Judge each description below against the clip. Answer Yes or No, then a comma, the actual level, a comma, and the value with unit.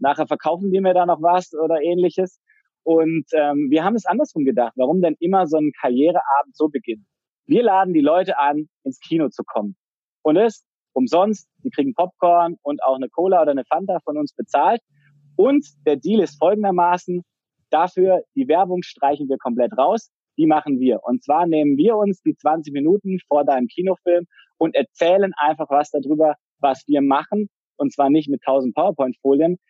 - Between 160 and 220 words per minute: Yes, average, 180 wpm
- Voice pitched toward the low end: No, medium, 160 Hz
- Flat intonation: No, average, 4.3 semitones